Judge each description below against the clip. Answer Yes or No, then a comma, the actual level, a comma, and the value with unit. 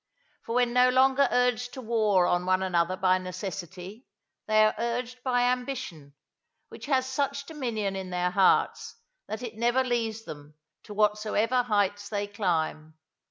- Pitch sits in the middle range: No, high, 215 Hz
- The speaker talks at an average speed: Yes, average, 155 wpm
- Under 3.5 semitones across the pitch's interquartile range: No, average, 5.0 semitones